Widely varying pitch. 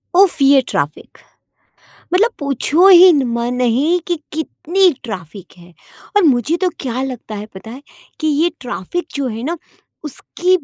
Yes: wide, 6.7 semitones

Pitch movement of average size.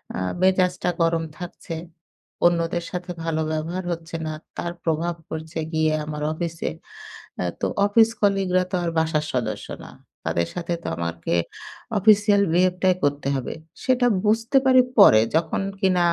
Yes: average, 3.0 semitones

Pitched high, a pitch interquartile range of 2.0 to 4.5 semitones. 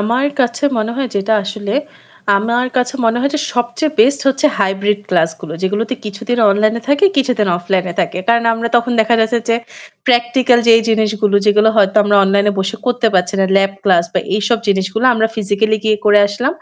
Yes: high, 220 Hz; average, 3.1 semitones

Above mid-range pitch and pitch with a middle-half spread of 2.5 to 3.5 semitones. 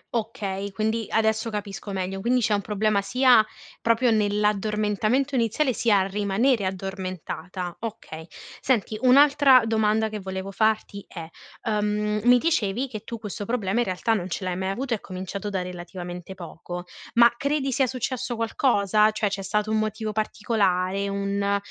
Yes: high, 210 Hz; average, 2.9 semitones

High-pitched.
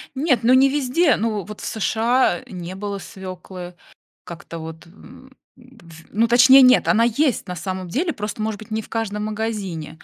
Yes: high, 215 Hz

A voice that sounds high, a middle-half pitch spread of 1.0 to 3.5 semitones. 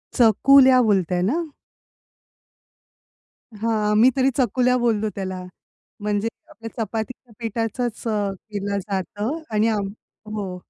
Yes: high, 220 Hz; average, 3.1 semitones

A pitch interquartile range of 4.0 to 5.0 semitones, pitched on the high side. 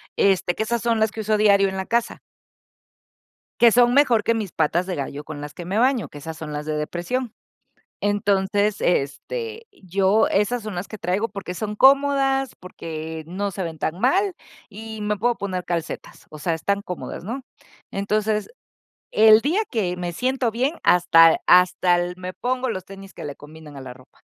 Yes: average, 4.7 semitones; high, 200 Hz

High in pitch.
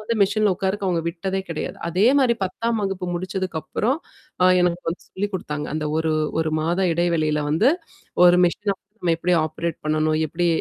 No: medium, 175 Hz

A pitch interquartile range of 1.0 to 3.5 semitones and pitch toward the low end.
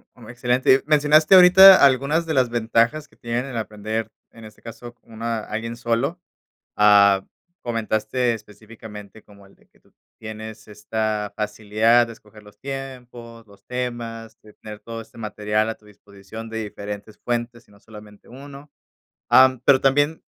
Yes: average, 2.9 semitones; low, 115 Hz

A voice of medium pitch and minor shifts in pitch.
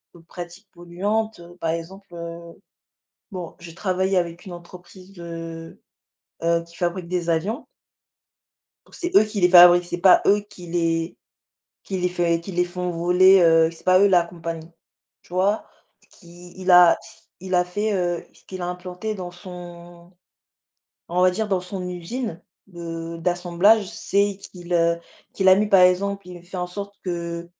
Yes: medium, 180 Hz; narrow, 1.8 semitones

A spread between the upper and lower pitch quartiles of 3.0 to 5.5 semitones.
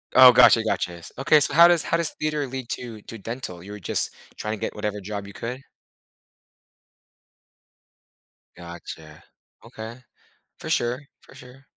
Yes: average, 4.6 semitones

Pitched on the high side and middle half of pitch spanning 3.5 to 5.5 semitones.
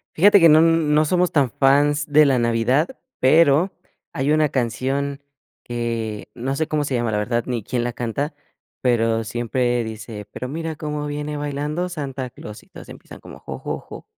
No: low, 135 Hz; average, 4.1 semitones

